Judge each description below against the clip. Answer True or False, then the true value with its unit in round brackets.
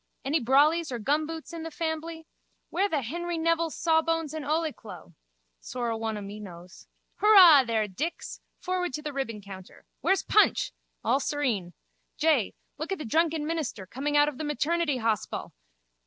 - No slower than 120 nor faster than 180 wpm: True (165 wpm)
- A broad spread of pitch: True (6.1 semitones)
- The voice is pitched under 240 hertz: False (295 Hz)